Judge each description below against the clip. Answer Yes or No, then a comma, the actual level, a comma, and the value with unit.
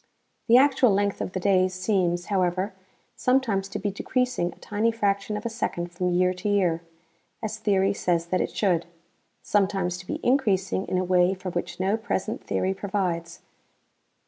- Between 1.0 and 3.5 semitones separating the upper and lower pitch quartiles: Yes, narrow, 2.4 semitones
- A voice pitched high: Yes, high, 195 Hz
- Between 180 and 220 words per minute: No, average, 170 wpm